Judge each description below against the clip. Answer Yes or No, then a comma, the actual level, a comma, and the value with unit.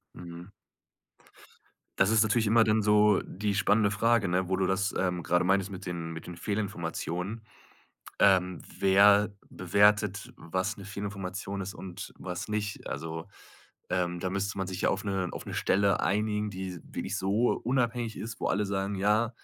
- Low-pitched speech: Yes, low, 100 Hz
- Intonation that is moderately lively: No, narrow, 2.2 semitones